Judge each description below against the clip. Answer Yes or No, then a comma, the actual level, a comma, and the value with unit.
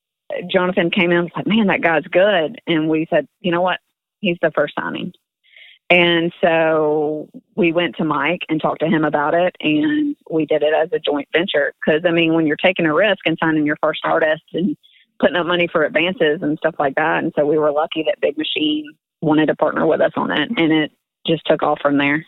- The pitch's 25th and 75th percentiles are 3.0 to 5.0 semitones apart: No, narrow, 2.5 semitones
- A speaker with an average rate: No, fast, 230 wpm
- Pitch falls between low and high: Yes, medium, 165 Hz